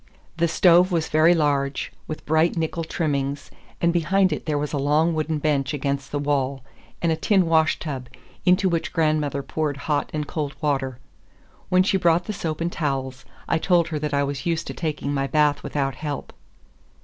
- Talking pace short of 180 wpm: No, average, 185 wpm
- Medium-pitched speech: Yes, medium, 155 Hz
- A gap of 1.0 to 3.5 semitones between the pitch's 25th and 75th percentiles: Yes, average, 2.8 semitones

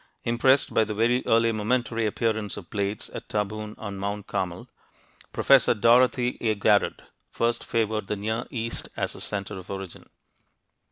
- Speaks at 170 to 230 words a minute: No, average, 155 wpm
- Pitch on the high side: No, low, 110 Hz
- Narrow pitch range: Yes, narrow, 2.3 semitones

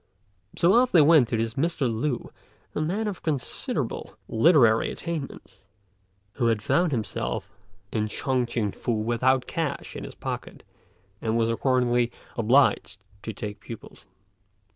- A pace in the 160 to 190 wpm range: No, average, 140 wpm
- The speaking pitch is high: No, low, 120 Hz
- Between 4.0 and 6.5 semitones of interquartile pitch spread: Yes, average, 5.2 semitones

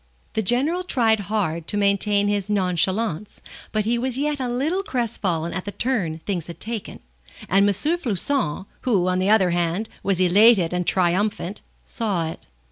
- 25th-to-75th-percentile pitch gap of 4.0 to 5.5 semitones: Yes, average, 4.4 semitones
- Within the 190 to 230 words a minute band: No, average, 165 wpm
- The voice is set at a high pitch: Yes, high, 205 Hz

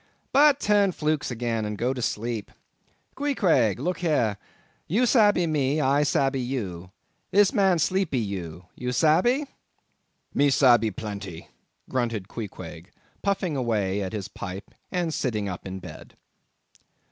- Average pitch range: No, wide, 8.8 semitones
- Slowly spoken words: Yes, slow, 120 wpm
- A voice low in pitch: Yes, low, 125 Hz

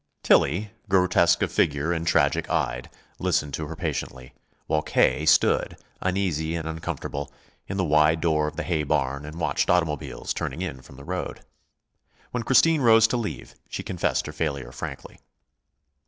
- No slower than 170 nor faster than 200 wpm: No, average, 160 wpm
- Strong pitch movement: No, average, 3.6 semitones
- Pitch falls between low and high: No, very low, 80 Hz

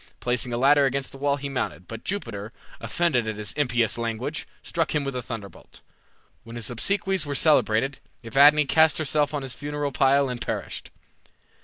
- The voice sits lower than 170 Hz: Yes, low, 135 Hz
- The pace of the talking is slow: No, average, 175 wpm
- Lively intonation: No, average, 3.9 semitones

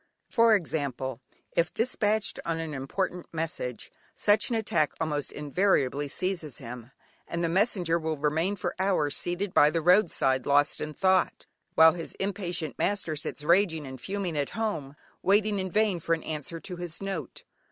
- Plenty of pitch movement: No, average, 4.6 semitones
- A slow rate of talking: No, average, 165 wpm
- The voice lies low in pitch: No, medium, 165 Hz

